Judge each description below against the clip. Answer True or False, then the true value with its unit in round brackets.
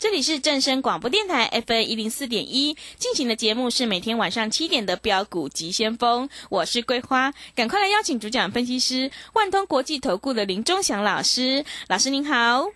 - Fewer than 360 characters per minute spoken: True (300 characters per minute)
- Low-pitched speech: False (255 Hz)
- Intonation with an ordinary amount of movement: True (4.7 semitones)